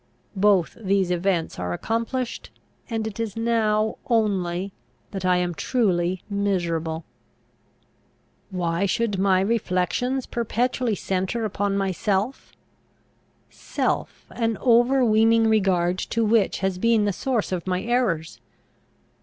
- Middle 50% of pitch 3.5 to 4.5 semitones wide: Yes, average, 3.8 semitones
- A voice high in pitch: Yes, high, 200 Hz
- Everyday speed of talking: No, slow, 110 wpm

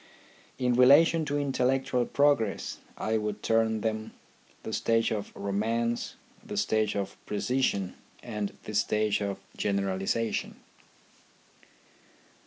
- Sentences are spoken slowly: Yes, slow, 105 wpm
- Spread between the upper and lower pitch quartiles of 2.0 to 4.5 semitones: Yes, average, 3.4 semitones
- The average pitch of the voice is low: Yes, low, 110 Hz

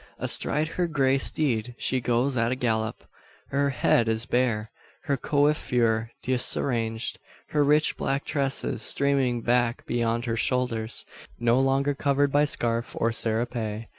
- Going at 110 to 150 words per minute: Yes, slow, 135 wpm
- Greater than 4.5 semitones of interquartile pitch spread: No, average, 3.2 semitones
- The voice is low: Yes, low, 125 Hz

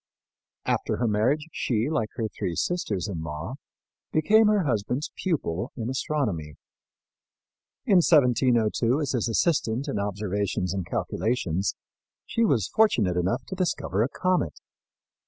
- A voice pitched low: Yes, low, 115 Hz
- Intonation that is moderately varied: No, wide, 6.9 semitones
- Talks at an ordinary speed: No, slow, 130 wpm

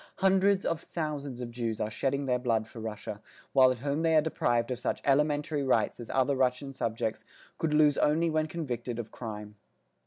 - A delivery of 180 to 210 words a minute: Yes, average, 190 wpm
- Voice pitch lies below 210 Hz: Yes, low, 135 Hz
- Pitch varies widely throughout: No, average, 4.5 semitones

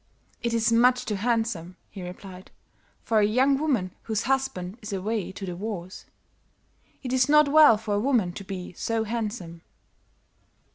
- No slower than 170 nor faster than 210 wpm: No, average, 160 wpm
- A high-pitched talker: Yes, high, 220 Hz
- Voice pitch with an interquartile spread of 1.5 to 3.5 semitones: No, average, 4.6 semitones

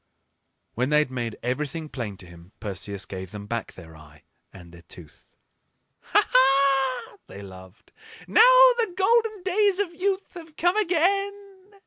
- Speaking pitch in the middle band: Yes, medium, 150 Hz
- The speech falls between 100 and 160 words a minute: Yes, average, 150 wpm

